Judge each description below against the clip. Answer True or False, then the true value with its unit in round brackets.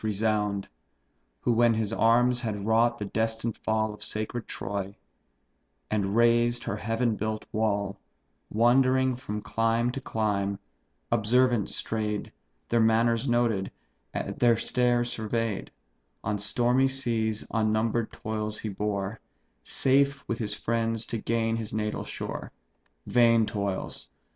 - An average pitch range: False (1.9 semitones)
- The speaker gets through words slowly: True (125 wpm)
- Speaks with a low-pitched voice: True (110 Hz)